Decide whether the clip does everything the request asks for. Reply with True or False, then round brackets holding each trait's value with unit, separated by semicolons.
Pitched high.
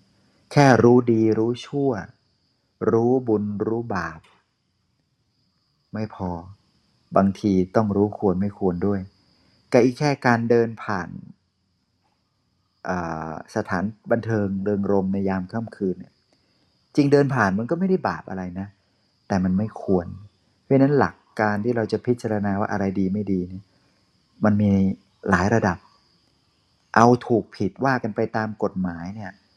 False (105 Hz)